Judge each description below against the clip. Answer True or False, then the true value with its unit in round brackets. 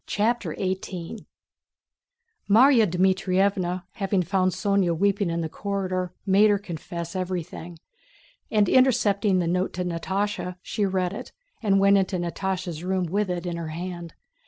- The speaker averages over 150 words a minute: False (140 wpm)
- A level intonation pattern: True (2.3 semitones)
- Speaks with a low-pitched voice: False (185 Hz)